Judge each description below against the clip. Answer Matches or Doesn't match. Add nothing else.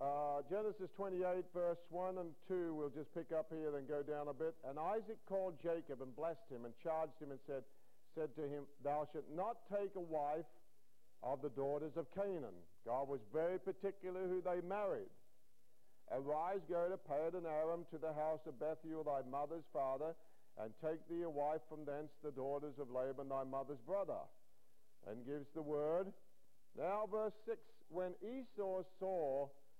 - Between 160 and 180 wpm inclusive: Matches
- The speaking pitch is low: Doesn't match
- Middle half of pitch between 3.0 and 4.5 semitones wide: Matches